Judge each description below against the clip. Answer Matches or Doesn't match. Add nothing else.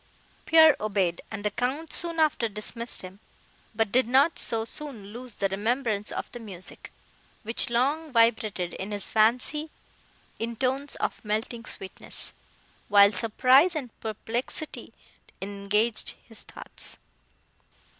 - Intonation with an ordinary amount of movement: Matches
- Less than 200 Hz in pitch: Doesn't match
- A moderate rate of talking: Doesn't match